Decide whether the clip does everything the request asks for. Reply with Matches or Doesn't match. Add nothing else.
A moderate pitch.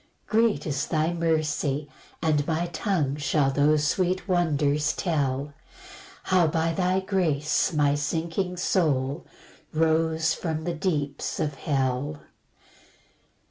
Matches